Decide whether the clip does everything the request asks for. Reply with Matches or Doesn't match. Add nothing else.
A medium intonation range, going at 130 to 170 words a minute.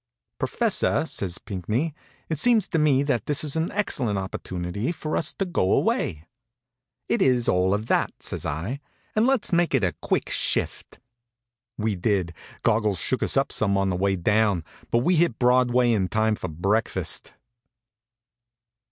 Doesn't match